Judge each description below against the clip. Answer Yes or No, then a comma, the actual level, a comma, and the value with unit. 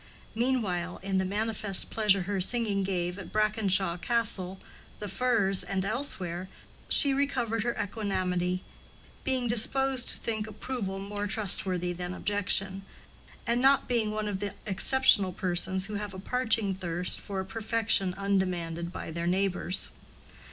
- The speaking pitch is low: No, high, 200 Hz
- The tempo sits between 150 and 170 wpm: No, average, 140 wpm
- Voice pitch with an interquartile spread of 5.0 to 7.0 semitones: No, average, 3.3 semitones